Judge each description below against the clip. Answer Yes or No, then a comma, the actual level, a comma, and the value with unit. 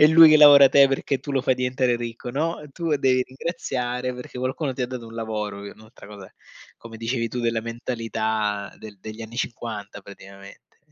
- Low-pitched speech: Yes, low, 120 Hz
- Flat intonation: No, average, 3.3 semitones